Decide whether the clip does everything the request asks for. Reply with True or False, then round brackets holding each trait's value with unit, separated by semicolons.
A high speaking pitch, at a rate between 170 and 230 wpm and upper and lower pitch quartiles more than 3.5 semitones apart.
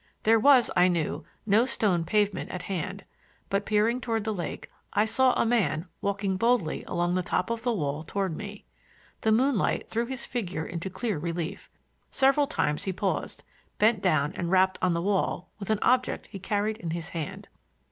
True (200 Hz; 185 wpm; 4.3 semitones)